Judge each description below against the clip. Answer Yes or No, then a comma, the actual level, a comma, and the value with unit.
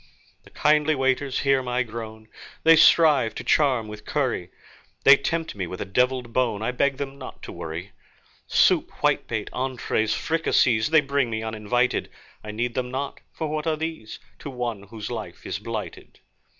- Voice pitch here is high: No, low, 125 Hz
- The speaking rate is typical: Yes, average, 170 wpm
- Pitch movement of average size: Yes, average, 4.3 semitones